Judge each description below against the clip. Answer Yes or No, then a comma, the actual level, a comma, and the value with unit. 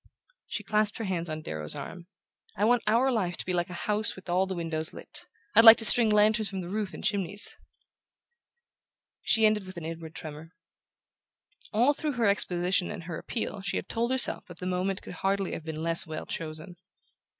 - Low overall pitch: No, high, 190 Hz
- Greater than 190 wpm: Yes, average, 200 wpm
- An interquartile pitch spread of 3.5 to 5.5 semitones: Yes, average, 4.0 semitones